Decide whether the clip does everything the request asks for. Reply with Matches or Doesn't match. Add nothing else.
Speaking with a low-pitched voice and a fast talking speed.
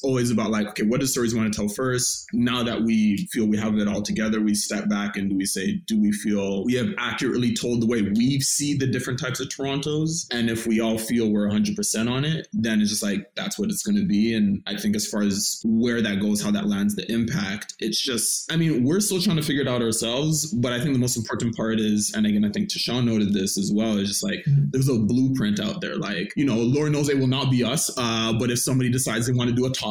Matches